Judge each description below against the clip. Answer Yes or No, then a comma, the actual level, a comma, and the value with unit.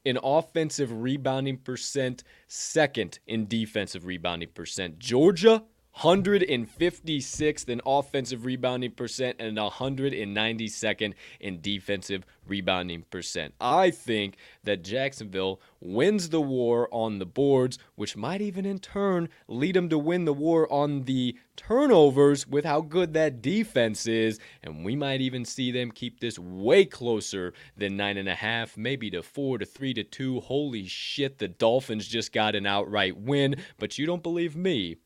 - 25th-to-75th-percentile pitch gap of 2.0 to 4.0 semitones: No, average, 5.2 semitones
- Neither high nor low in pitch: No, low, 125 Hz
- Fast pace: No, average, 150 wpm